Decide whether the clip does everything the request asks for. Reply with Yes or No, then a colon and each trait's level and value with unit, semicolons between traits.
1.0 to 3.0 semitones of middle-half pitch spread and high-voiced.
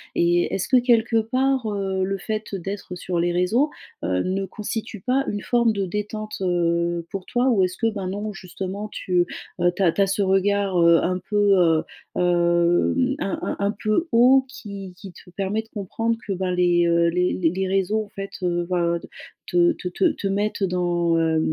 No: average, 3.4 semitones; high, 195 Hz